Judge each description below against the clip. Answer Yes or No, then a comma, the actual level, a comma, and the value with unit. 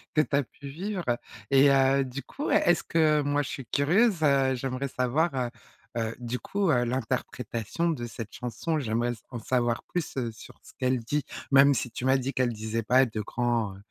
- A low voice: Yes, low, 130 Hz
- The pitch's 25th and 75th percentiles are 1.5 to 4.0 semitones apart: Yes, average, 3.2 semitones